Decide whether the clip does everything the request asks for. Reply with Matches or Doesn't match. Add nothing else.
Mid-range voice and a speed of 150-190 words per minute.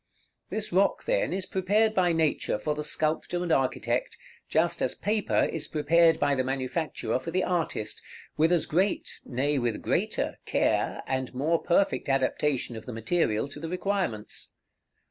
Matches